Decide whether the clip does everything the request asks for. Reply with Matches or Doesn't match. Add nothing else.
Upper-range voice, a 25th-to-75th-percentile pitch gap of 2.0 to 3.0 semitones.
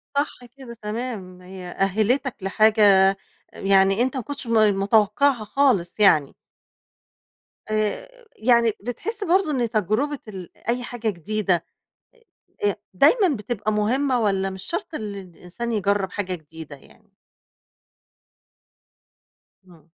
Doesn't match